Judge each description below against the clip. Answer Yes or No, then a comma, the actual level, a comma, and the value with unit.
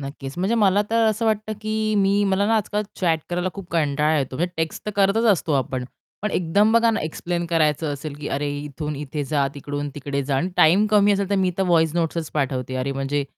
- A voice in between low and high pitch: Yes, medium, 165 Hz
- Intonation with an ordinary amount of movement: No, wide, 5.7 semitones